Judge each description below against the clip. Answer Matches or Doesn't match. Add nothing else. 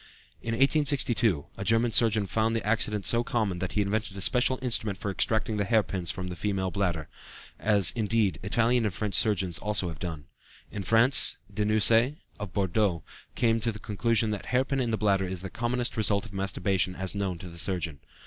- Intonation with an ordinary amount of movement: Matches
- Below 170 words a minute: Doesn't match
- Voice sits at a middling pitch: Doesn't match